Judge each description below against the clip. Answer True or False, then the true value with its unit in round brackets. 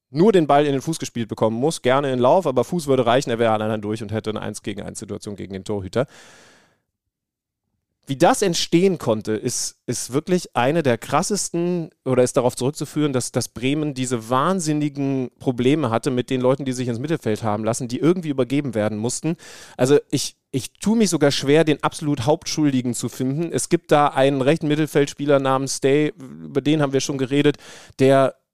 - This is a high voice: False (135 Hz)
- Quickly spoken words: True (195 wpm)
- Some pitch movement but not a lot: True (3.9 semitones)